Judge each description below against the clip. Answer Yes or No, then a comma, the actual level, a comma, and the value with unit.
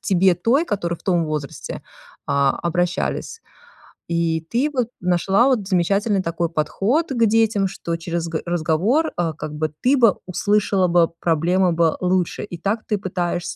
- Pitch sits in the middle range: Yes, medium, 180 Hz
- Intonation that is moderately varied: Yes, average, 3.8 semitones